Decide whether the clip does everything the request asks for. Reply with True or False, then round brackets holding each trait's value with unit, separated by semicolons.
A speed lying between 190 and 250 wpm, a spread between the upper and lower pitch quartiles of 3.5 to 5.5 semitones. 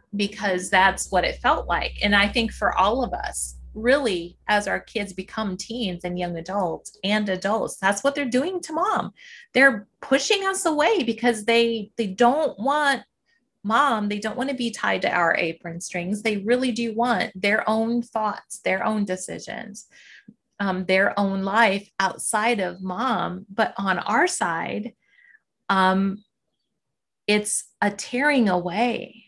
False (155 wpm; 3.8 semitones)